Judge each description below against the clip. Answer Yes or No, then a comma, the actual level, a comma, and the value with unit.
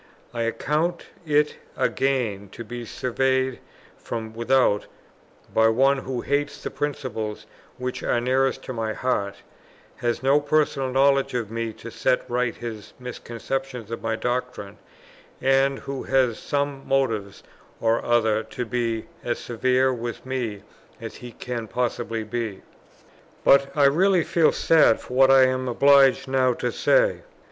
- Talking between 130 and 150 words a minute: Yes, average, 145 wpm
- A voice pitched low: Yes, low, 125 Hz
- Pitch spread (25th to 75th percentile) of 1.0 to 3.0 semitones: Yes, average, 2.7 semitones